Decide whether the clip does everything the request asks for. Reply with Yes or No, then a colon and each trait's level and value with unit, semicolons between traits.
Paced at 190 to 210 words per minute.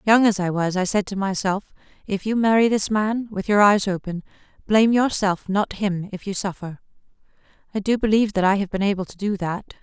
Yes: average, 200 wpm